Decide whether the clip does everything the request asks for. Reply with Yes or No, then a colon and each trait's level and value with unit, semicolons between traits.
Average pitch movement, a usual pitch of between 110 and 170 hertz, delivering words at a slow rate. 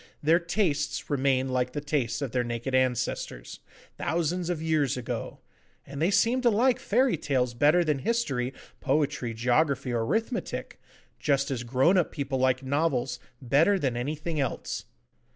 No: average, 4.6 semitones; medium, 140 Hz; average, 150 wpm